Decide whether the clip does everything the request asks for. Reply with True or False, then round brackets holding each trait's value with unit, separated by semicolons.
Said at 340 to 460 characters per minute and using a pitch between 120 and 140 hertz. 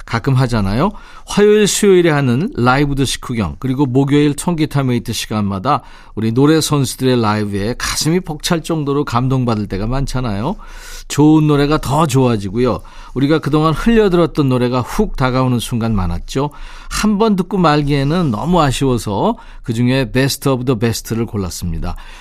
True (365 characters per minute; 135 Hz)